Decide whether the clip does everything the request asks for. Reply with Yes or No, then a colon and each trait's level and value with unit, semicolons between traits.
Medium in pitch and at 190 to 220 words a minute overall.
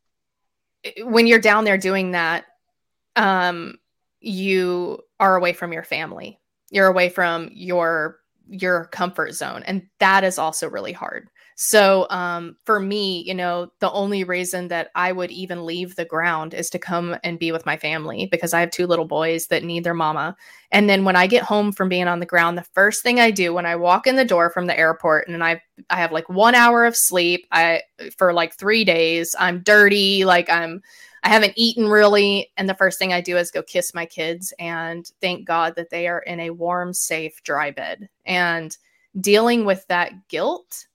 Yes: medium, 180 Hz; average, 200 wpm